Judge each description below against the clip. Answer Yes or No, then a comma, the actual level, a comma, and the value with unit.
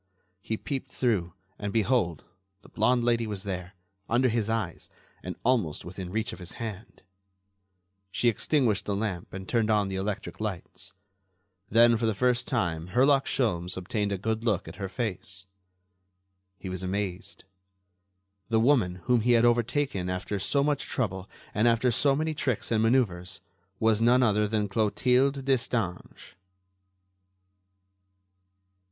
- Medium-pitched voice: No, low, 110 Hz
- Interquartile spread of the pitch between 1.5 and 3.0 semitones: No, average, 4.1 semitones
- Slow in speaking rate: No, average, 145 wpm